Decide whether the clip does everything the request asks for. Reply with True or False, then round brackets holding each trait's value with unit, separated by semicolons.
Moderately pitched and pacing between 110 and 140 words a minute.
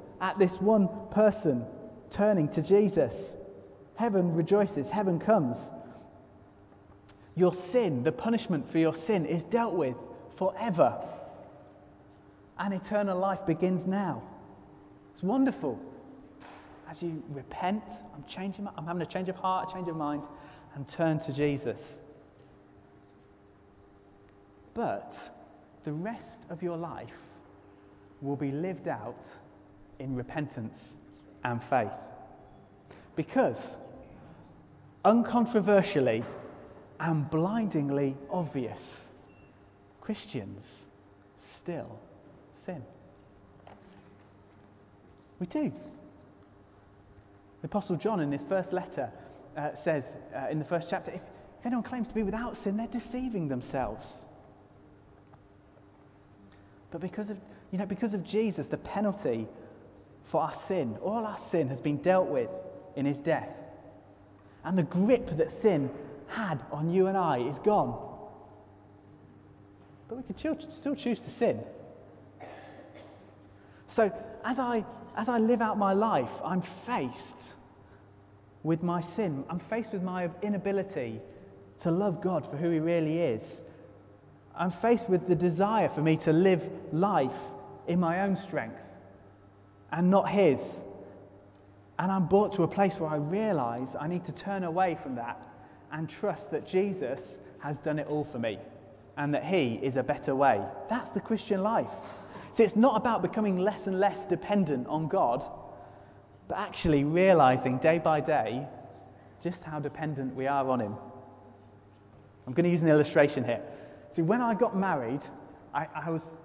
True (155 Hz; 135 wpm)